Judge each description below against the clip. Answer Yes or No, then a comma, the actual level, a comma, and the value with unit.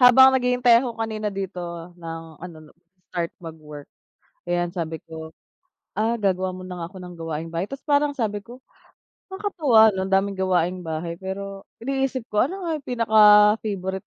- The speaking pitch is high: Yes, high, 195 Hz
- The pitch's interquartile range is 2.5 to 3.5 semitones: No, wide, 5.5 semitones